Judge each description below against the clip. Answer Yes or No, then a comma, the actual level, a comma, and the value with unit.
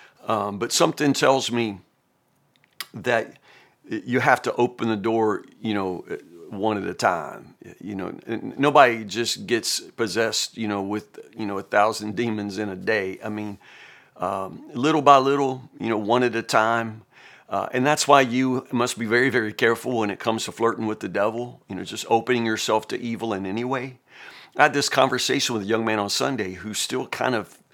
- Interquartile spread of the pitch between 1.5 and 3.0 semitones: Yes, average, 2.7 semitones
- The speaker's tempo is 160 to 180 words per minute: No, average, 195 wpm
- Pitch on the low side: Yes, low, 115 Hz